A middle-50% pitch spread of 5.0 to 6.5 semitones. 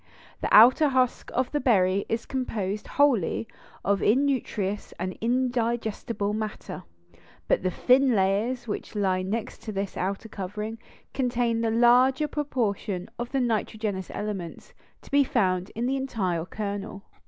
No: average, 4.0 semitones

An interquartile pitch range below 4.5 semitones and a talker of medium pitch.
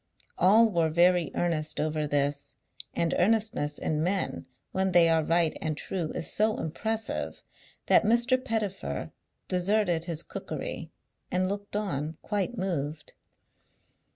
No: average, 4.8 semitones; medium, 175 Hz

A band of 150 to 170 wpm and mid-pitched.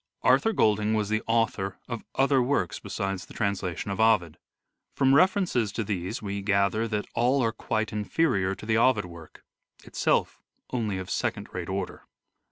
No: average, 165 wpm; low, 105 Hz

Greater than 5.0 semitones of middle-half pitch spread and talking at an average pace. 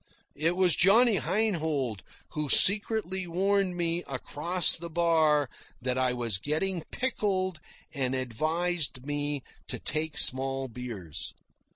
No: wide, 5.6 semitones; slow, 115 wpm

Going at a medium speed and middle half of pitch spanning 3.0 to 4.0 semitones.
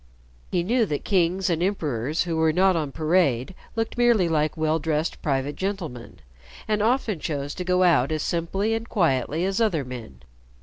No: average, 175 wpm; average, 4.5 semitones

